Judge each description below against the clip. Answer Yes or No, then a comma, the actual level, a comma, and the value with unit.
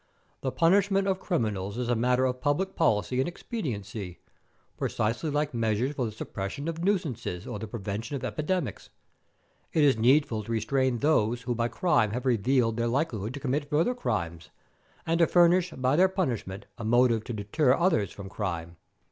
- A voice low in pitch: Yes, low, 125 Hz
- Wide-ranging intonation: Yes, wide, 6.1 semitones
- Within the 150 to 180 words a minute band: Yes, average, 175 wpm